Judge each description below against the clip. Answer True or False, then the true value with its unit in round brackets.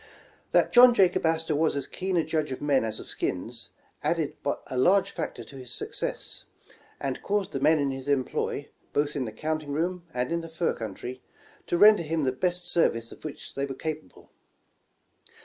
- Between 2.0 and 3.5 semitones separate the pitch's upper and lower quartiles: False (4.4 semitones)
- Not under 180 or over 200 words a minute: True (190 wpm)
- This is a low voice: False (155 Hz)